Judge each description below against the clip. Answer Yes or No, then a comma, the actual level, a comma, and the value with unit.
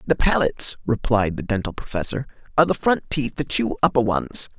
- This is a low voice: Yes, low, 125 Hz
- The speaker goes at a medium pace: Yes, average, 185 wpm